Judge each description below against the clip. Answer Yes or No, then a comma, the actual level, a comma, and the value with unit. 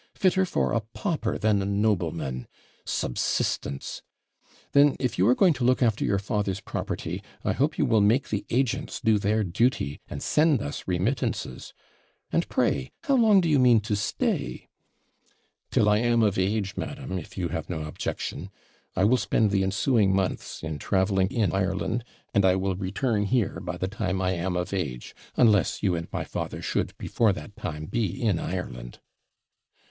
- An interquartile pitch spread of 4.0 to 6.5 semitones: Yes, average, 4.3 semitones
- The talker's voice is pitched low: Yes, low, 100 Hz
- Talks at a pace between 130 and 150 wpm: No, average, 175 wpm